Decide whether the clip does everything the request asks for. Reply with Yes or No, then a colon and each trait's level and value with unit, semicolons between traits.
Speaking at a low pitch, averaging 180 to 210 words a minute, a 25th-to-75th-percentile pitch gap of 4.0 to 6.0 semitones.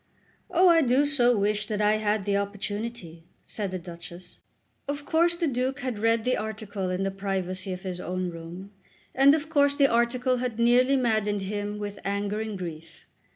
No: high, 210 Hz; average, 185 wpm; average, 4.6 semitones